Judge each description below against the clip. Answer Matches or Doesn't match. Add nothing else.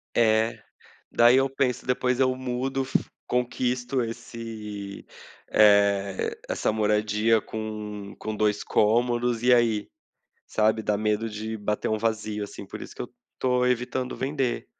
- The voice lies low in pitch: Matches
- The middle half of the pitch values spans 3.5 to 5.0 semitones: Doesn't match